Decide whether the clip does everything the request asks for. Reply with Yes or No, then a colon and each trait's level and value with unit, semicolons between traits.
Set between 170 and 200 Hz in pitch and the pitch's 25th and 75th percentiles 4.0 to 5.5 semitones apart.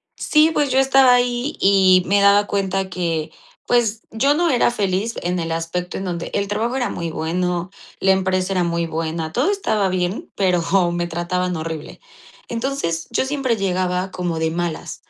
Yes: medium, 185 Hz; average, 4.9 semitones